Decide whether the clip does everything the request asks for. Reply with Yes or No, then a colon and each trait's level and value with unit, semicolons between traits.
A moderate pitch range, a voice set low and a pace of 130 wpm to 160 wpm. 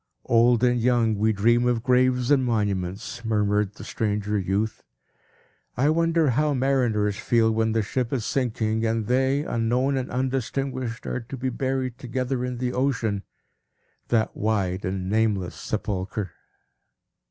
Yes: average, 3.2 semitones; low, 115 Hz; average, 140 wpm